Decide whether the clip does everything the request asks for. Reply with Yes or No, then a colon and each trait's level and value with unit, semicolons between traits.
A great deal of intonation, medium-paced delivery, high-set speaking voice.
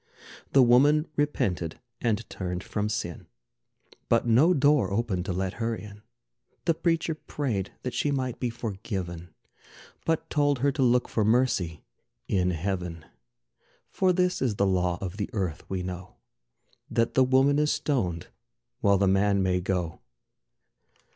No: wide, 6.4 semitones; average, 150 wpm; low, 110 Hz